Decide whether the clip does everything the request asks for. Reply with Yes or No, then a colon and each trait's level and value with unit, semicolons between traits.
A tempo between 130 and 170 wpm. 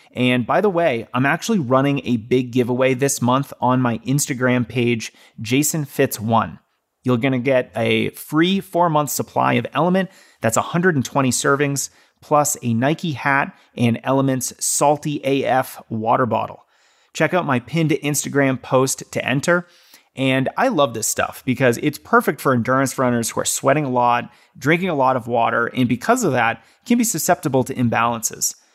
Yes: average, 165 wpm